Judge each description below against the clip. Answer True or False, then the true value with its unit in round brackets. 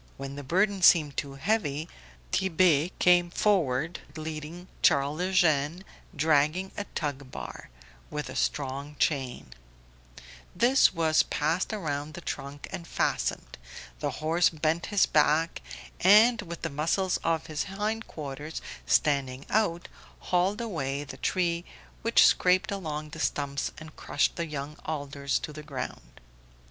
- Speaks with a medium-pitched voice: True (155 Hz)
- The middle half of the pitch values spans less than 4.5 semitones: True (3.9 semitones)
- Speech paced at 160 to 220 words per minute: False (135 wpm)